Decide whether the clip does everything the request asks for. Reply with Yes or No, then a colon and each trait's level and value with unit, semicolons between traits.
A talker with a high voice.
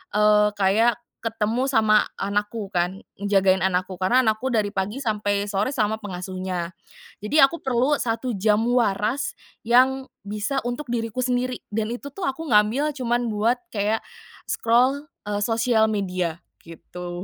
Yes: high, 215 Hz